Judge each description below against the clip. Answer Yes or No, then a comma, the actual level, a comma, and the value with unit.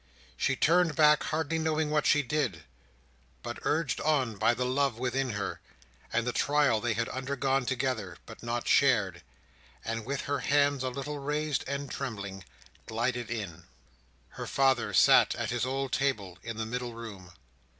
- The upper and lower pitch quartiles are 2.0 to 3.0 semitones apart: No, average, 3.7 semitones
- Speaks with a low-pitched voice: Yes, low, 130 Hz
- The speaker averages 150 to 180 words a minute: Yes, average, 160 wpm